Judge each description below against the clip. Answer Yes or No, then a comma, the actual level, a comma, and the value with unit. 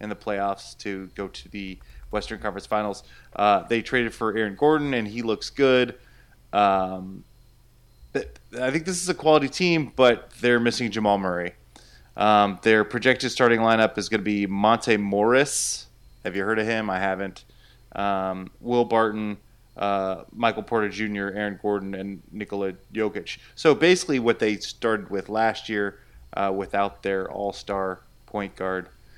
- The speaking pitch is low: Yes, low, 105 Hz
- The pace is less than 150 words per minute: No, average, 160 wpm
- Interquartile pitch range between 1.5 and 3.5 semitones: Yes, average, 2.9 semitones